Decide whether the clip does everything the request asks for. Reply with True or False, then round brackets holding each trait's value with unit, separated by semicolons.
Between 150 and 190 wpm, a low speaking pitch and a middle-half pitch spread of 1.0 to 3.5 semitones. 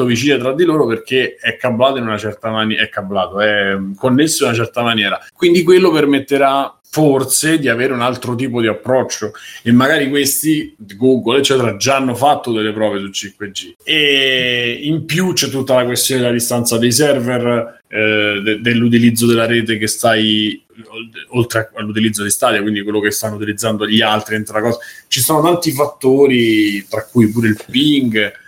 False (170 wpm; 120 Hz; 4.1 semitones)